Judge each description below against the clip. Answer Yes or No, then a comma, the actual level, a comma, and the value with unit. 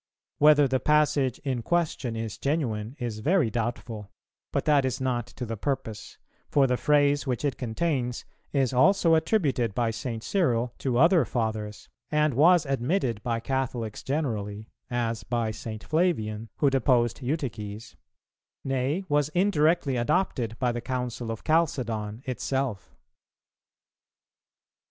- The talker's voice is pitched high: No, low, 125 Hz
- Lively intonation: No, average, 4.4 semitones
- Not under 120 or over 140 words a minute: Yes, slow, 135 wpm